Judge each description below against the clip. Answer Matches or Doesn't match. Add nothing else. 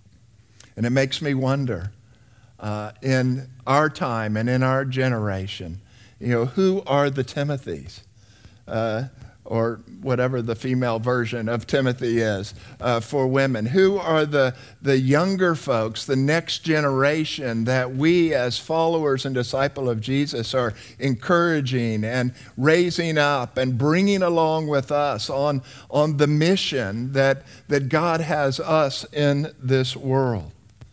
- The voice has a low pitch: Matches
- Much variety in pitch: Doesn't match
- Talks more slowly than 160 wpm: Matches